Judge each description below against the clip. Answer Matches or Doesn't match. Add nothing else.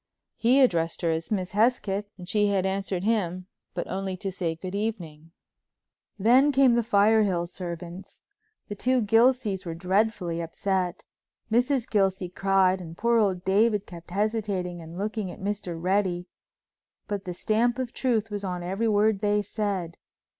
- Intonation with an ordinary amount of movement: Matches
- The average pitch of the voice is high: Matches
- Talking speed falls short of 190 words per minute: Matches